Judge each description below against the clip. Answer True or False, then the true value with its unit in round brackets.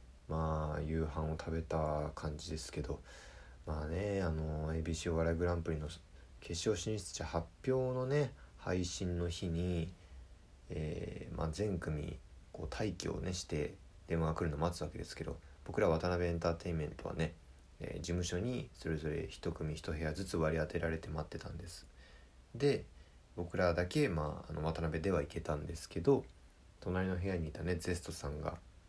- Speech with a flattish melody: True (2.3 semitones)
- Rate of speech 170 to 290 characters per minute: False (315 characters per minute)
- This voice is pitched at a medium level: False (85 Hz)